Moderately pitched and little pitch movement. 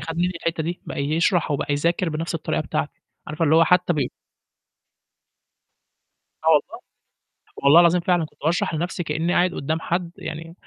Yes: medium, 165 Hz; narrow, 2.0 semitones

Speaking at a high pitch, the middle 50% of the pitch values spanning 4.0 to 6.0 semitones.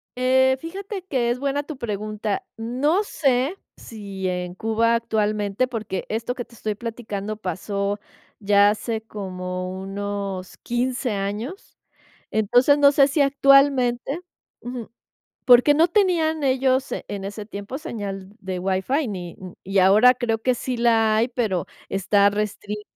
Yes: high, 225 Hz; average, 4.4 semitones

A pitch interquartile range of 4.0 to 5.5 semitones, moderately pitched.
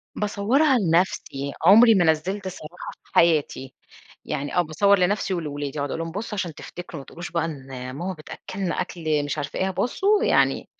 Yes: average, 4.4 semitones; medium, 175 Hz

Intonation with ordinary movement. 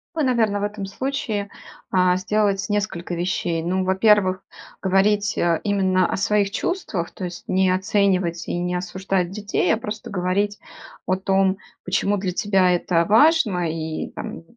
No: narrow, 2.3 semitones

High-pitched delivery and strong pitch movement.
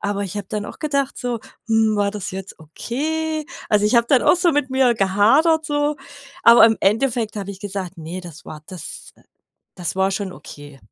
Yes: high, 210 Hz; wide, 5.9 semitones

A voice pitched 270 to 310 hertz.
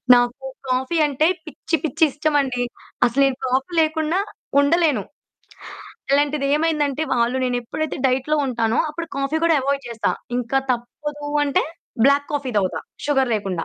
Yes: very high, 275 Hz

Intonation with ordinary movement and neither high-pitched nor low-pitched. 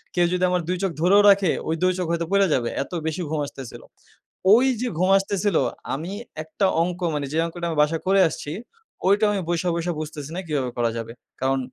Yes: average, 4.2 semitones; medium, 170 Hz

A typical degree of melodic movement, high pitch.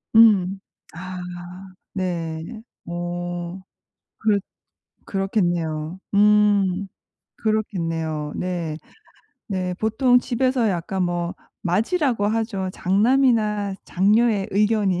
Yes: average, 3.6 semitones; high, 195 Hz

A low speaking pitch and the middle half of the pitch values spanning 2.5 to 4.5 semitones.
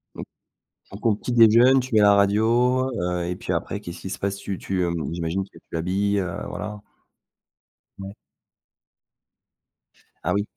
Yes: low, 100 Hz; average, 3.2 semitones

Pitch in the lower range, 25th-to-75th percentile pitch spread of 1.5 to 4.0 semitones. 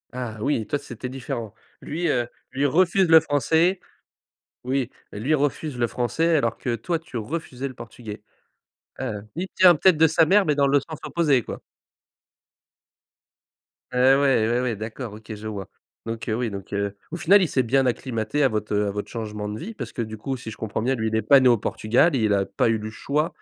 No: low, 125 Hz; average, 5.2 semitones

